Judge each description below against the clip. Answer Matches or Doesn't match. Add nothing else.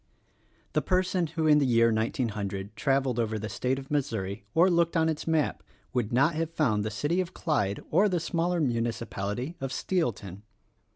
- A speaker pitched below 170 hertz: Matches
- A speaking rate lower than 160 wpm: Doesn't match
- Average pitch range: Doesn't match